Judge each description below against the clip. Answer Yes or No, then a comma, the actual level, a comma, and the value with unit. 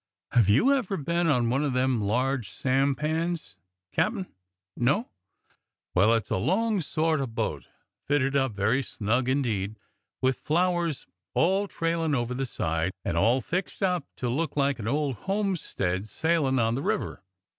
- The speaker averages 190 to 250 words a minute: No, average, 155 wpm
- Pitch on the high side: No, low, 135 Hz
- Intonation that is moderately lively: No, wide, 6.1 semitones